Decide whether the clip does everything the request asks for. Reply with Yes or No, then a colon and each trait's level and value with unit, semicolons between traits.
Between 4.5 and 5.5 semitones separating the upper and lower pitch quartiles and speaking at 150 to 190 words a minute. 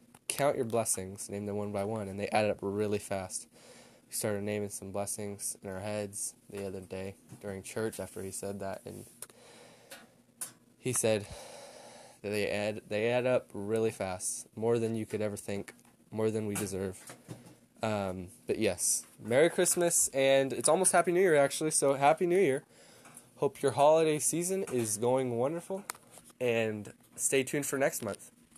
Yes: average, 5.0 semitones; average, 170 wpm